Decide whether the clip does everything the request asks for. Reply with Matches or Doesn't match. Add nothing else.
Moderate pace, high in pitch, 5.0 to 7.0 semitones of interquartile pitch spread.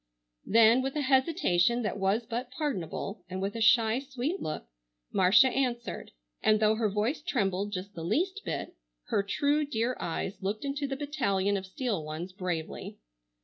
Matches